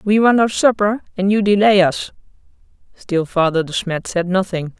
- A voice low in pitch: No, high, 195 Hz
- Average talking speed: Yes, average, 175 wpm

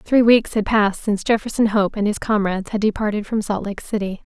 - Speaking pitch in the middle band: No, high, 210 Hz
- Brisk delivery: Yes, fast, 220 wpm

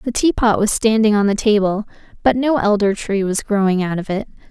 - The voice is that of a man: No, female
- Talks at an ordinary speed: No, fast, 225 wpm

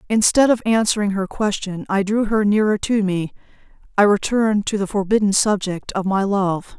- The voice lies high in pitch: Yes, high, 205 Hz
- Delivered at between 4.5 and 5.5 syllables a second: Yes, 5.1 syllables/s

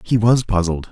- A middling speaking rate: Yes, average, 195 wpm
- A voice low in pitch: Yes, low, 105 Hz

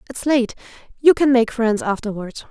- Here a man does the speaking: No, female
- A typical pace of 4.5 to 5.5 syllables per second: Yes, 4.8 syllables/s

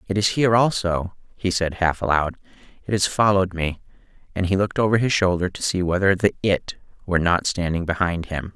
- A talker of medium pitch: No, very low, 95 Hz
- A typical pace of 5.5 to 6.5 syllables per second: Yes, 5.8 syllables/s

